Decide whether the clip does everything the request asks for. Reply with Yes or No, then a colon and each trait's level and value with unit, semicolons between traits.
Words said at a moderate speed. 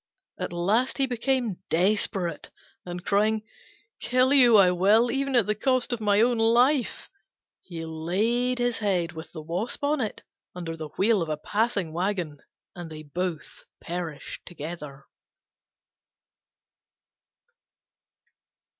No: slow, 130 wpm